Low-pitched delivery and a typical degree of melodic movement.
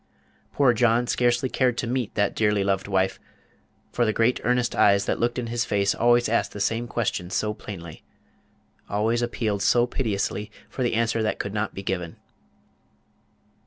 Yes: low, 115 Hz; average, 3.0 semitones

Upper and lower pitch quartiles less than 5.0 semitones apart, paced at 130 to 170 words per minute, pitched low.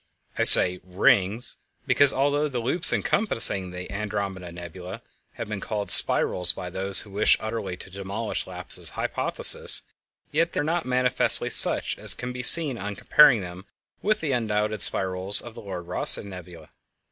No: average, 5.3 semitones; average, 160 wpm; low, 105 Hz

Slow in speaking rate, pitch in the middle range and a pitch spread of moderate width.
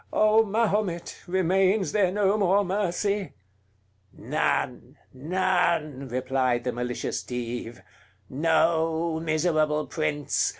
Yes: slow, 90 wpm; medium, 170 Hz; average, 5.0 semitones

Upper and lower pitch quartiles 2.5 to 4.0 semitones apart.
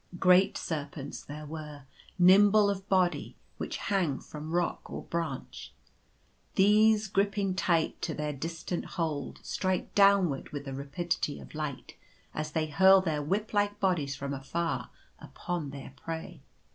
No: average, 4.6 semitones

